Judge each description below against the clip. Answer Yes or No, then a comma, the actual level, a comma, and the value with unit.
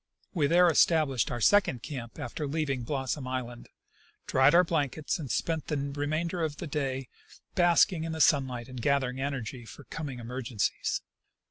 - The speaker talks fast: No, average, 155 wpm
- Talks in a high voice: No, medium, 140 Hz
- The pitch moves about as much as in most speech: Yes, average, 3.7 semitones